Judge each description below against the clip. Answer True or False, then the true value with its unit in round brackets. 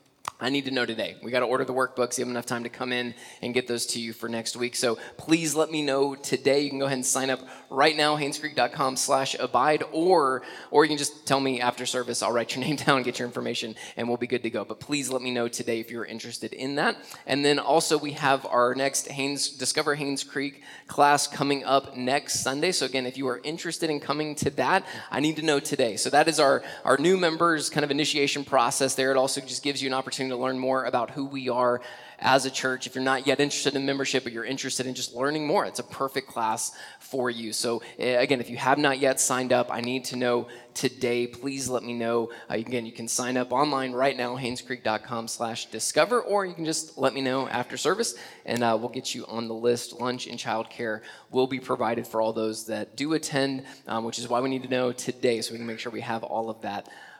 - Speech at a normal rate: False (250 wpm)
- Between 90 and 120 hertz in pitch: False (130 Hz)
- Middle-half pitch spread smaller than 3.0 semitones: True (2.5 semitones)